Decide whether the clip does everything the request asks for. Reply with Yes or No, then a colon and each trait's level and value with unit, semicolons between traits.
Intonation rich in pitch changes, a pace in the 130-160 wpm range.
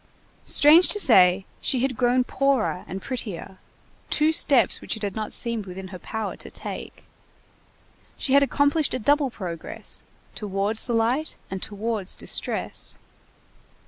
Yes: wide, 5.8 semitones; average, 145 wpm